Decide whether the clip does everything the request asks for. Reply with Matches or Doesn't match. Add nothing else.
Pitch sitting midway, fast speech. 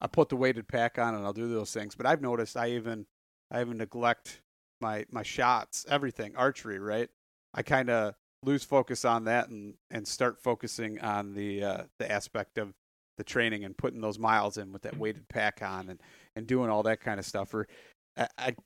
Doesn't match